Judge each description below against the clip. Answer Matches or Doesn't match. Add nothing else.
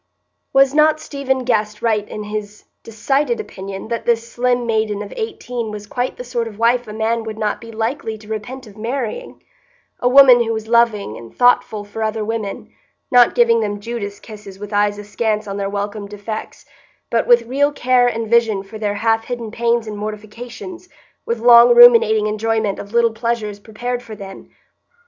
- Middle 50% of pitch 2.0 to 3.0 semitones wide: Matches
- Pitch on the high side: Matches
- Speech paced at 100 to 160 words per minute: Doesn't match